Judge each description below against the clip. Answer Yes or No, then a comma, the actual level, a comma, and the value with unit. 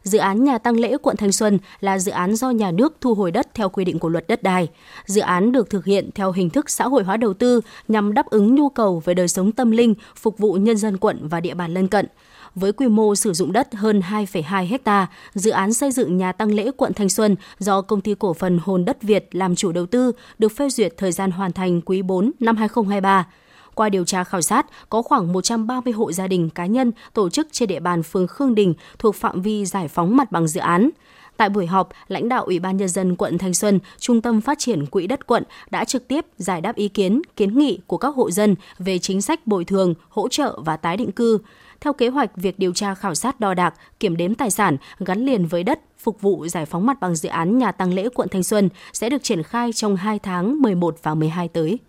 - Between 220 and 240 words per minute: No, fast, 250 wpm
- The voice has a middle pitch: No, high, 205 Hz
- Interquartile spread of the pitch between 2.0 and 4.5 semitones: Yes, average, 4.0 semitones